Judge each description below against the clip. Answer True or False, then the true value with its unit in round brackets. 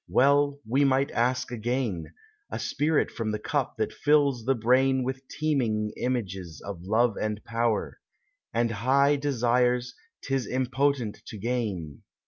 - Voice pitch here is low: True (125 Hz)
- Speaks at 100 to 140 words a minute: True (135 wpm)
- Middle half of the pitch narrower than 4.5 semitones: True (3.6 semitones)